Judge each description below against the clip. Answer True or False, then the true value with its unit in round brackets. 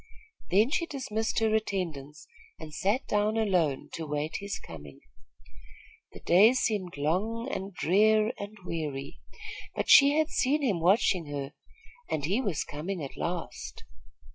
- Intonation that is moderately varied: False (5.9 semitones)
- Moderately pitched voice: False (195 Hz)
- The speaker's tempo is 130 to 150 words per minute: True (140 wpm)